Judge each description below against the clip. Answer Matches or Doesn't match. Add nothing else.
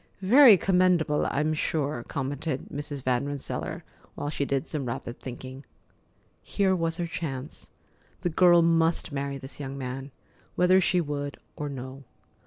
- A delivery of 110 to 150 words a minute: Matches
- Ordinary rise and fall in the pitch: Matches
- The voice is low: Doesn't match